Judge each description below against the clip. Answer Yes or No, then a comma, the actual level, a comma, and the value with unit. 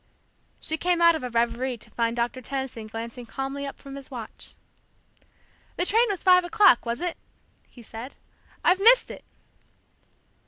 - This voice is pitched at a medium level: No, very high, 270 Hz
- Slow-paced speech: No, average, 160 wpm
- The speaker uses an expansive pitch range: Yes, wide, 6.8 semitones